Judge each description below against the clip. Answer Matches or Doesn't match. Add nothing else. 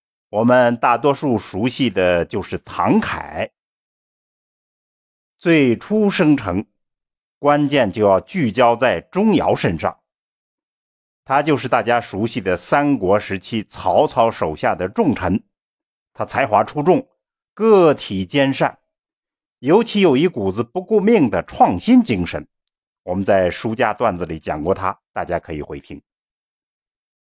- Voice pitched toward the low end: Matches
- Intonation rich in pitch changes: Matches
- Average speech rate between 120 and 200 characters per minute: Matches